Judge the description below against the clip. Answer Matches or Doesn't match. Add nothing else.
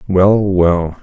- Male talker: Matches